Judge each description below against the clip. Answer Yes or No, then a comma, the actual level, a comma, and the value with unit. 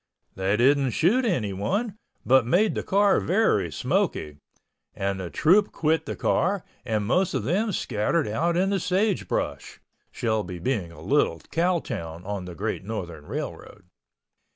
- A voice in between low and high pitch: No, low, 125 Hz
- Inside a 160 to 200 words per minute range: No, average, 150 wpm